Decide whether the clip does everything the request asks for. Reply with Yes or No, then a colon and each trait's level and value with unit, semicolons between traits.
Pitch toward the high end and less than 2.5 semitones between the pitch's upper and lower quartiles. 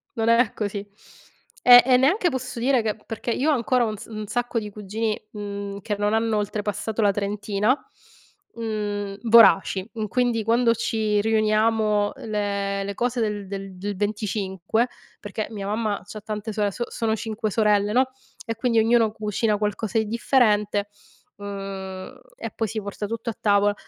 Yes: high, 215 Hz; narrow, 2.0 semitones